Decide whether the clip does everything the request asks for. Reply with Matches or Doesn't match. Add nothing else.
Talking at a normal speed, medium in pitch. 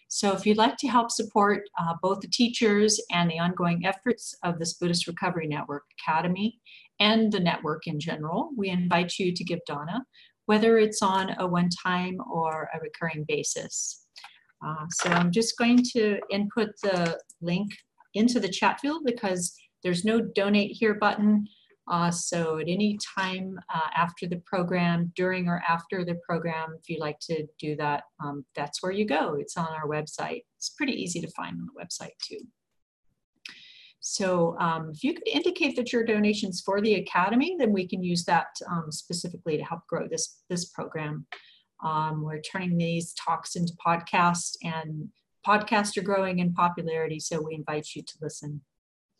Matches